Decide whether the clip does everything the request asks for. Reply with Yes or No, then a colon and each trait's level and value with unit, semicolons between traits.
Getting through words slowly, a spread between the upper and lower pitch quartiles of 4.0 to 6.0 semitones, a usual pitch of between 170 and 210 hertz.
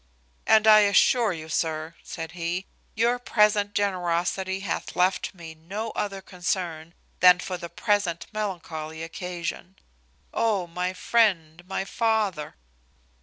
No: slow, 125 wpm; average, 3.5 semitones; medium, 185 Hz